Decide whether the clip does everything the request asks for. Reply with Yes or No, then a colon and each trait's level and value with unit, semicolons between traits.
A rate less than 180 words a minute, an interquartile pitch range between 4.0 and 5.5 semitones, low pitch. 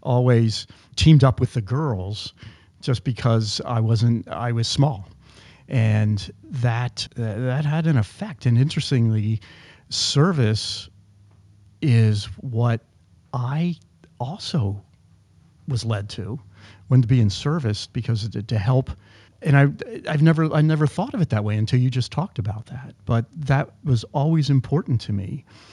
Yes: average, 145 wpm; average, 4.6 semitones; low, 115 Hz